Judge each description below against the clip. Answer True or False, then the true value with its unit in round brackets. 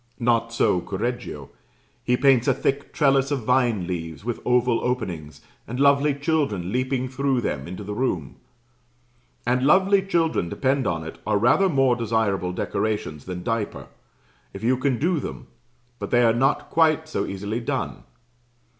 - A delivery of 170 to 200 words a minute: False (155 wpm)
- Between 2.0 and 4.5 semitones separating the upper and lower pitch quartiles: False (5.0 semitones)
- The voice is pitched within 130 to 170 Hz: False (120 Hz)